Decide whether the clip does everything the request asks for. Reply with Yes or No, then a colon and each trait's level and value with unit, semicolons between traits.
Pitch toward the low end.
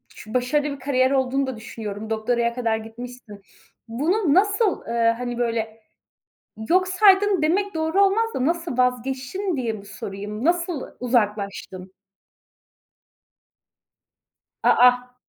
No: very high, 250 Hz